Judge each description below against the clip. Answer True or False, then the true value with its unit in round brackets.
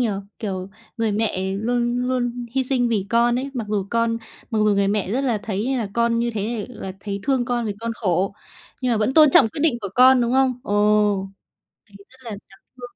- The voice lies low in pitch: False (230 Hz)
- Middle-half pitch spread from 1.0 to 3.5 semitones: True (3.1 semitones)